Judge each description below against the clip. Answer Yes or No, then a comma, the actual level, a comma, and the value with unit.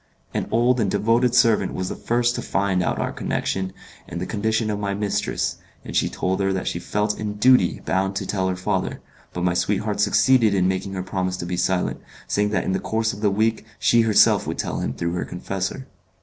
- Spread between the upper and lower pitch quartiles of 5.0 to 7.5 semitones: No, average, 2.8 semitones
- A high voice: No, low, 100 Hz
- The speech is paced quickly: Yes, fast, 220 wpm